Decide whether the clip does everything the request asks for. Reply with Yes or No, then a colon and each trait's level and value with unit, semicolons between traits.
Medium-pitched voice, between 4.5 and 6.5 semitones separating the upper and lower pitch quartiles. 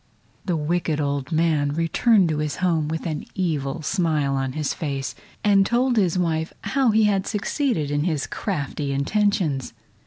Yes: medium, 160 Hz; average, 4.9 semitones